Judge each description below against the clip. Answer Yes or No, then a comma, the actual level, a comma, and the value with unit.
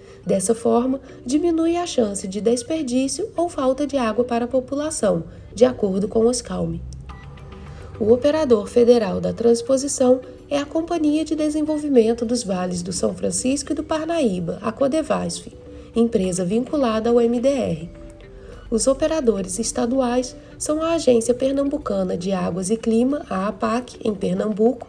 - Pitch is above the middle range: Yes, high, 245 Hz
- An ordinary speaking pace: Yes, average, 140 wpm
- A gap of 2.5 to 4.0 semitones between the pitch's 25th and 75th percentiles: No, average, 4.6 semitones